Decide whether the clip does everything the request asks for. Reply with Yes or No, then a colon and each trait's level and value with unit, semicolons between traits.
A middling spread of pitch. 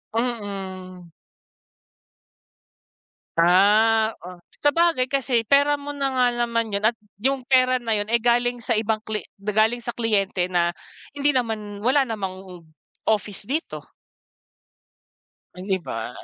Yes: average, 4.2 semitones